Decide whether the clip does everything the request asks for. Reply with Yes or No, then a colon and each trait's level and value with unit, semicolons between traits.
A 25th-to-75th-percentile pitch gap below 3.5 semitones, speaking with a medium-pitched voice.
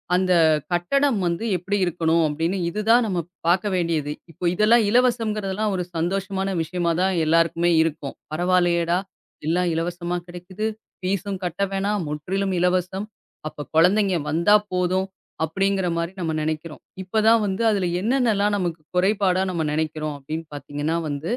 Yes: average, 3.1 semitones; medium, 180 Hz